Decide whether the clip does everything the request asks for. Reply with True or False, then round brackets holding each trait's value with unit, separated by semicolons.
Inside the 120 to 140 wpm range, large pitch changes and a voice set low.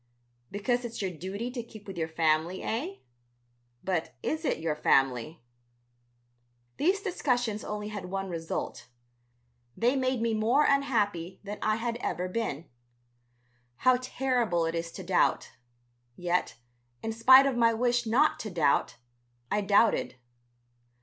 False (135 wpm; 5.7 semitones; 215 Hz)